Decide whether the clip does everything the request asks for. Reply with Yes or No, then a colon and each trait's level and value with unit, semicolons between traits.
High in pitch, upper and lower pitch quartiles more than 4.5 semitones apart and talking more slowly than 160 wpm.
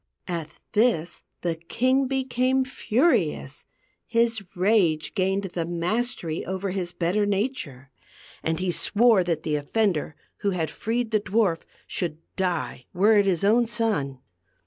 Yes: high, 195 Hz; average, 5.2 semitones; average, 150 wpm